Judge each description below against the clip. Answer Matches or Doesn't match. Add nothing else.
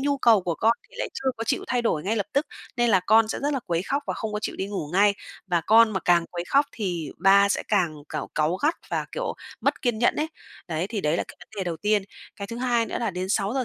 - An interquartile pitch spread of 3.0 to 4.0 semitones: Doesn't match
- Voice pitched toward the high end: Matches